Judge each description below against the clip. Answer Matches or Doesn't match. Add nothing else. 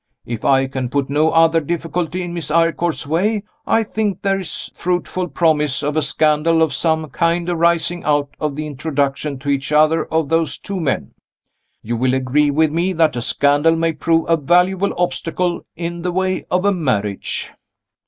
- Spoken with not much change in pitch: Doesn't match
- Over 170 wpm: Matches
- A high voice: Doesn't match